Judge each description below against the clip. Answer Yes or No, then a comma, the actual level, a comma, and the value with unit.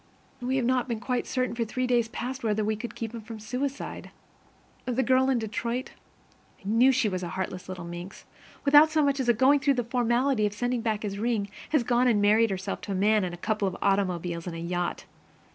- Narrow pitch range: No, average, 4.0 semitones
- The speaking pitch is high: Yes, high, 230 Hz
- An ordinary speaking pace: No, fast, 225 wpm